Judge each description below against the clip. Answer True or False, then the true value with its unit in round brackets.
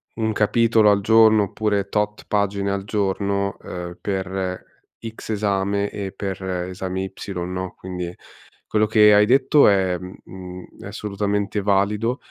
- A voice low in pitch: True (100 Hz)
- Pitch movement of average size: False (1.9 semitones)